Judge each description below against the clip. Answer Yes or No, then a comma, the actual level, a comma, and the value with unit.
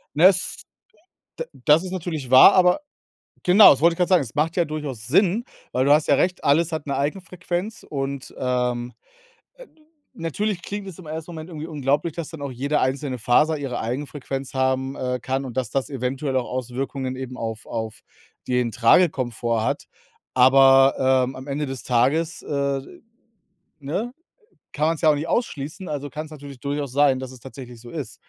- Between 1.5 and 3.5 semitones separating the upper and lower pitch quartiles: No, average, 4.0 semitones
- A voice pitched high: No, medium, 140 Hz